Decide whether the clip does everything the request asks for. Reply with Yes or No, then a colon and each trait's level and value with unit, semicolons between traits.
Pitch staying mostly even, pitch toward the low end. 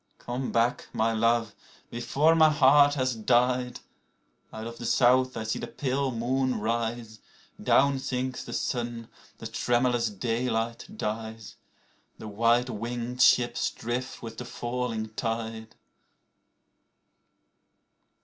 Yes: narrow, 2.0 semitones; low, 120 Hz